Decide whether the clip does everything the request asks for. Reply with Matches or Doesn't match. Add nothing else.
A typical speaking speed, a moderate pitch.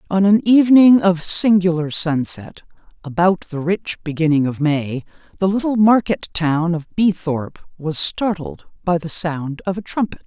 Matches